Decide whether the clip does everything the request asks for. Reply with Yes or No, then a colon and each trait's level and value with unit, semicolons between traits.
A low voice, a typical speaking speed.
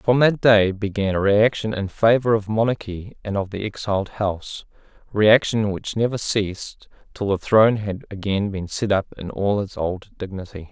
Yes: low, 105 Hz; average, 180 wpm